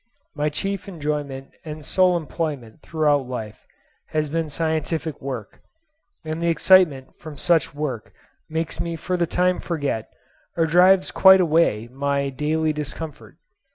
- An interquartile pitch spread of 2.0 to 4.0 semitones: Yes, average, 2.9 semitones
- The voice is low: No, medium, 155 Hz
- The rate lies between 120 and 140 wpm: Yes, slow, 135 wpm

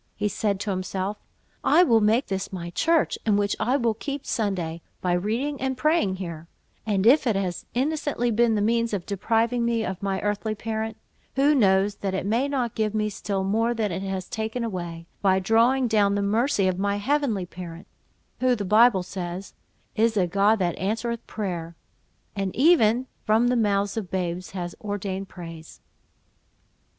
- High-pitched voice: Yes, high, 210 Hz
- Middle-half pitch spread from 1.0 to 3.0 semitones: No, average, 3.6 semitones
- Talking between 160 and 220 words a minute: Yes, average, 175 wpm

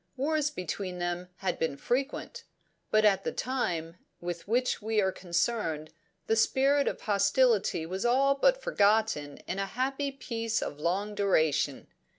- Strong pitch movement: Yes, wide, 6.5 semitones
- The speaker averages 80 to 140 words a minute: No, average, 150 wpm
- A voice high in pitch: Yes, high, 210 Hz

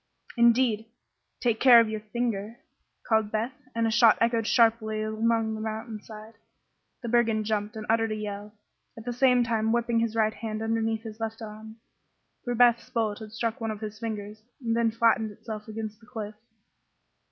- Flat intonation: Yes, narrow, 1.2 semitones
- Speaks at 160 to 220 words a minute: Yes, average, 180 wpm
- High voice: Yes, high, 225 Hz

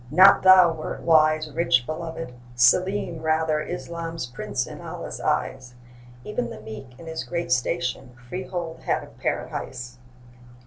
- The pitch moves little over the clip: No, average, 5.2 semitones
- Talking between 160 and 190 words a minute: No, slow, 135 wpm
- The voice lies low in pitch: No, medium, 160 Hz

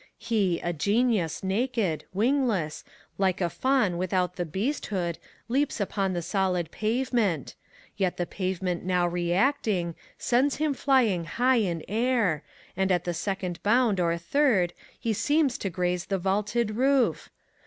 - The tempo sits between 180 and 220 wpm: No, average, 140 wpm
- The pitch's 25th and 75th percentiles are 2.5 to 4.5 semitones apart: No, average, 5.3 semitones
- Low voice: No, high, 195 Hz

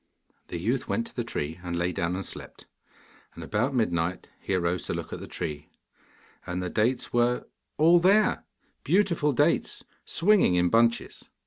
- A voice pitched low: Yes, low, 110 Hz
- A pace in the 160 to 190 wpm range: Yes, average, 165 wpm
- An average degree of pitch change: No, wide, 8.7 semitones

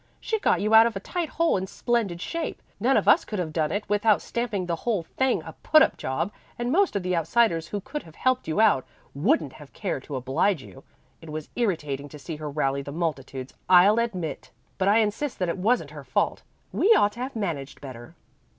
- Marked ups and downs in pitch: Yes, wide, 7.3 semitones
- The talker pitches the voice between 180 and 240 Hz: Yes, medium, 185 Hz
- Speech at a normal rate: No, fast, 225 wpm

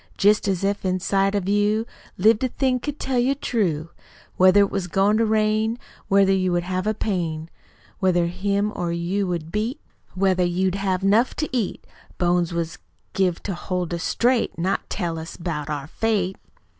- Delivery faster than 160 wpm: Yes, average, 180 wpm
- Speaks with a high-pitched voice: Yes, high, 195 Hz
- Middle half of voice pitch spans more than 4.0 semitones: No, average, 3.3 semitones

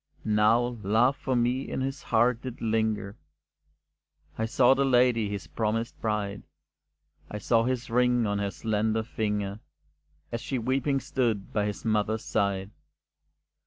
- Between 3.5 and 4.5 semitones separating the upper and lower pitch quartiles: No, average, 2.8 semitones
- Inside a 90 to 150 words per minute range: Yes, average, 140 wpm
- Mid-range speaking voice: No, low, 115 Hz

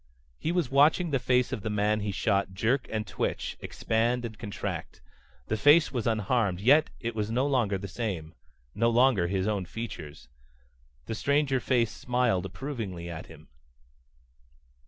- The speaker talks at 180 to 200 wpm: No, average, 155 wpm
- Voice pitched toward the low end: Yes, low, 115 Hz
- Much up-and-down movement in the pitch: No, average, 4.5 semitones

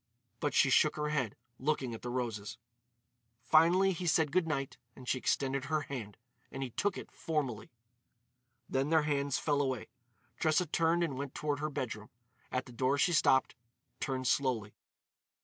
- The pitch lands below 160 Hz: Yes, medium, 140 Hz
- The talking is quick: No, average, 165 wpm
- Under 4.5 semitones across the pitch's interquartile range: Yes, average, 3.2 semitones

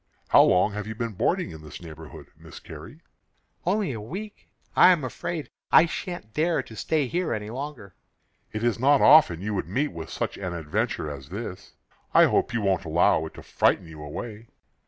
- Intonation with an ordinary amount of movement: No, wide, 8.7 semitones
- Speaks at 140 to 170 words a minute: No, average, 195 wpm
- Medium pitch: No, low, 110 Hz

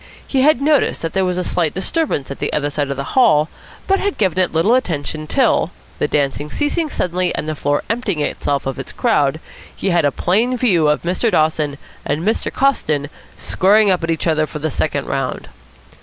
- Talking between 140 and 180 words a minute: No, fast, 205 wpm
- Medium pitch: Yes, medium, 165 Hz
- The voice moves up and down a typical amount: No, wide, 6.7 semitones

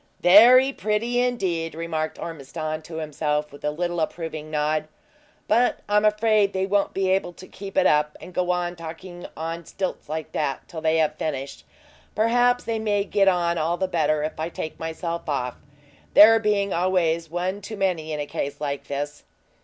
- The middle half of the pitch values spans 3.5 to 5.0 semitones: Yes, average, 4.2 semitones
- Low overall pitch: No, medium, 170 Hz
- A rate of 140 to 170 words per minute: No, average, 180 wpm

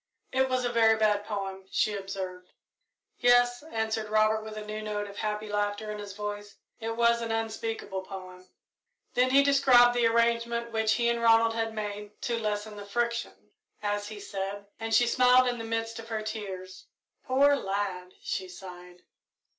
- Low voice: No, high, 220 Hz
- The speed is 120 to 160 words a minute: No, average, 175 wpm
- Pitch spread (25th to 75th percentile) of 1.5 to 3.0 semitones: Yes, narrow, 2.4 semitones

